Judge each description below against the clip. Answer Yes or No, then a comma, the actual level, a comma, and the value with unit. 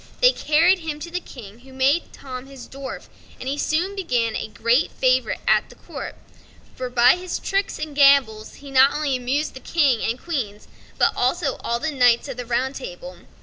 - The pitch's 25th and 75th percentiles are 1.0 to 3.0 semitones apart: No, average, 3.9 semitones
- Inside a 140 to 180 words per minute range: No, average, 190 wpm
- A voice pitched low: No, very high, 270 Hz